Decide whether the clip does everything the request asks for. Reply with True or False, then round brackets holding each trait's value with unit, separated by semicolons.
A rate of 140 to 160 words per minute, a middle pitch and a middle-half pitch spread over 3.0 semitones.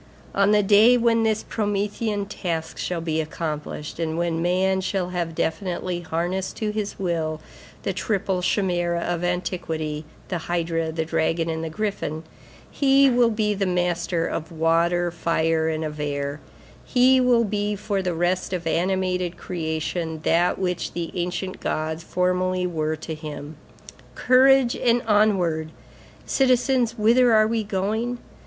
True (150 wpm; 180 Hz; 4.2 semitones)